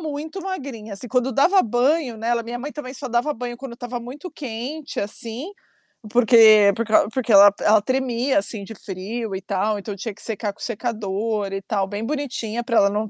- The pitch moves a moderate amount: Yes, average, 3.7 semitones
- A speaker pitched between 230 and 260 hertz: Yes, high, 235 Hz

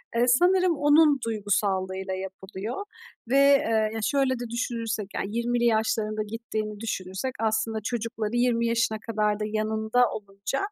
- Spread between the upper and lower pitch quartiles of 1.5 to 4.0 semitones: Yes, narrow, 2.4 semitones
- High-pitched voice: Yes, high, 225 Hz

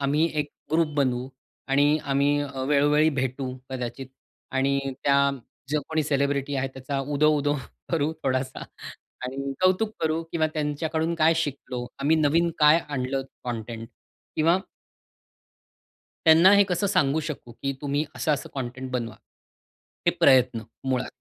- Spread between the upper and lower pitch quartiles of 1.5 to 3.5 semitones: Yes, average, 2.9 semitones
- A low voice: No, medium, 145 Hz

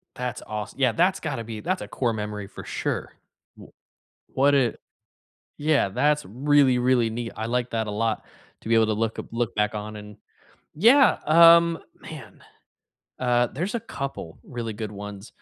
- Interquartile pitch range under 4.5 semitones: No, average, 4.9 semitones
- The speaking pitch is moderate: No, low, 120 Hz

